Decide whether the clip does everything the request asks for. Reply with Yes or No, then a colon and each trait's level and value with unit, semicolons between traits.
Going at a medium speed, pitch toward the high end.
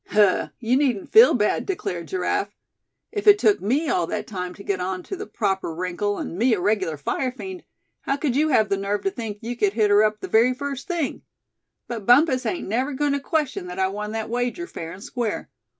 No: fast, 225 wpm; high, 220 Hz